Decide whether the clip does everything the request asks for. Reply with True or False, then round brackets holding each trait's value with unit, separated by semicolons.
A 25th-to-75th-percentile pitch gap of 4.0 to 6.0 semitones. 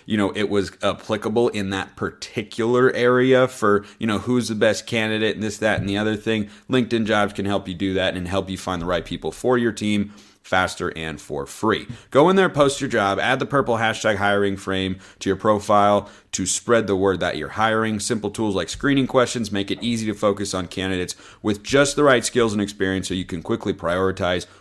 False (3.1 semitones)